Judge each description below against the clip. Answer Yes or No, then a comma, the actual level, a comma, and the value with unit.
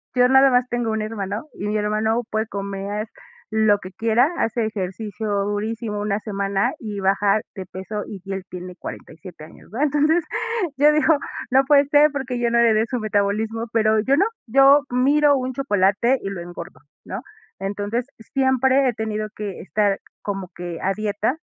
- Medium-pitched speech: No, high, 220 Hz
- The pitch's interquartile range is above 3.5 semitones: Yes, average, 4.0 semitones